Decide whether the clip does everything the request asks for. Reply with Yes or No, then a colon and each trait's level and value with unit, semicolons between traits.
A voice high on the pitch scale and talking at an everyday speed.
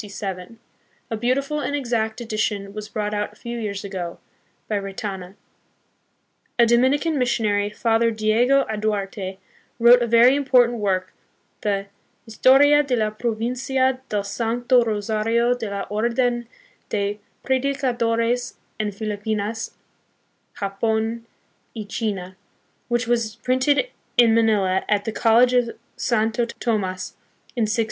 No: high, 225 Hz; slow, 125 wpm